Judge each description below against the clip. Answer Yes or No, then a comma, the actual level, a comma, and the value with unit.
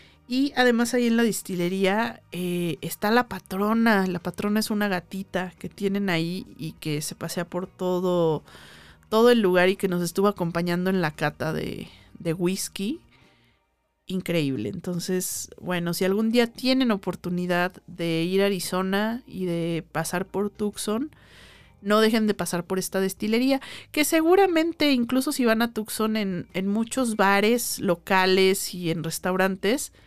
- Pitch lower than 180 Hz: No, high, 190 Hz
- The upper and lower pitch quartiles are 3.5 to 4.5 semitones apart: Yes, average, 3.8 semitones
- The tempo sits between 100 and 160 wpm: Yes, average, 155 wpm